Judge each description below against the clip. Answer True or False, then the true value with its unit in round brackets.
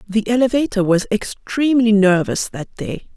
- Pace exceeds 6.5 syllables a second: False (5.1 syllables/s)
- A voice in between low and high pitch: False (210 Hz)